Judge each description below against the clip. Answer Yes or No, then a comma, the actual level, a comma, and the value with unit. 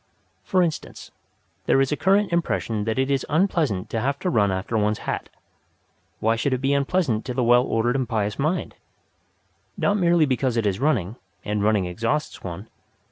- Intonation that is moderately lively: No, wide, 5.8 semitones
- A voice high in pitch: No, low, 125 Hz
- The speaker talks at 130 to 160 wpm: No, average, 185 wpm